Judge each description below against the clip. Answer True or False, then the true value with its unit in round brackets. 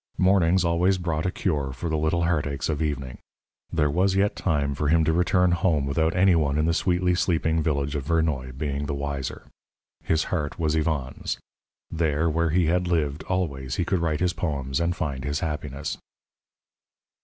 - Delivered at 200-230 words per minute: False (180 wpm)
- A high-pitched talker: False (80 Hz)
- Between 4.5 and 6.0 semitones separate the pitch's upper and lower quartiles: False (3.2 semitones)